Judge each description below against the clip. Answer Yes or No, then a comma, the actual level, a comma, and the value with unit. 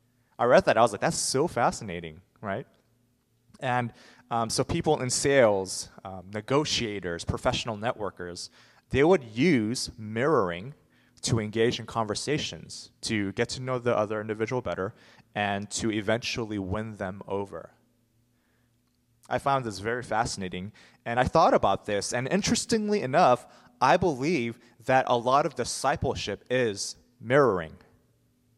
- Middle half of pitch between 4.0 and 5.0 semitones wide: No, average, 3.0 semitones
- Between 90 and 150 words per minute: Yes, slow, 135 wpm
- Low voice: Yes, low, 115 Hz